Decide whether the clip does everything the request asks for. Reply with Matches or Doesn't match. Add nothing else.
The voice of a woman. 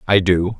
Doesn't match